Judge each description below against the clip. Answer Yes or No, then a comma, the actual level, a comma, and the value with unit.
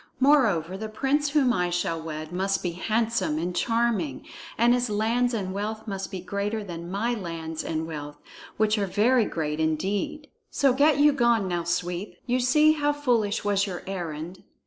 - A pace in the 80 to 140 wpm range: No, average, 175 wpm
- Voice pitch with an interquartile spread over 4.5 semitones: Yes, wide, 5.6 semitones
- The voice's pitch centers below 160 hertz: No, high, 205 Hz